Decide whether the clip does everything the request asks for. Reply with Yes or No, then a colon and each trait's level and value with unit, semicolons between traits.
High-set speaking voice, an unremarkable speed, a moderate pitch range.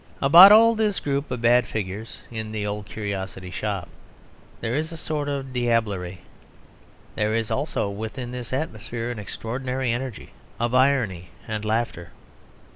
No: low, 115 Hz; average, 145 wpm; average, 4.1 semitones